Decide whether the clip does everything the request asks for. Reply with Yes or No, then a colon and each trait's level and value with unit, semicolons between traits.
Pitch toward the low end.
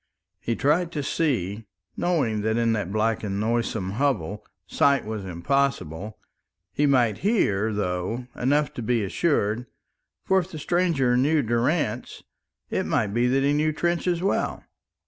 Yes: low, 120 Hz